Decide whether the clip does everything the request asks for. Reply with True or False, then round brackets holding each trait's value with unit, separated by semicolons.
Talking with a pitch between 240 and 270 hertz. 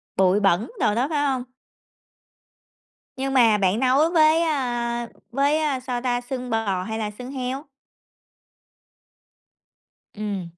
True (245 Hz)